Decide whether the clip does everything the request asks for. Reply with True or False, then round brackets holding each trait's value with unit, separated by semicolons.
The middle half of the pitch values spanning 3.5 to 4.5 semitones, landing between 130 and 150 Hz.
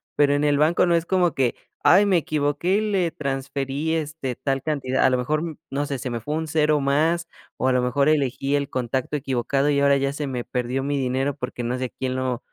False (2.8 semitones; 140 Hz)